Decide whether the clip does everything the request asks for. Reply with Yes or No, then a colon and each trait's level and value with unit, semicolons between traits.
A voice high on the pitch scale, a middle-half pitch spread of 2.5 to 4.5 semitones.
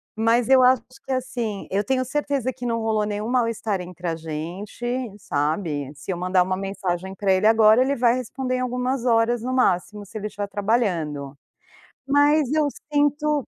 No: high, 220 Hz; average, 5.2 semitones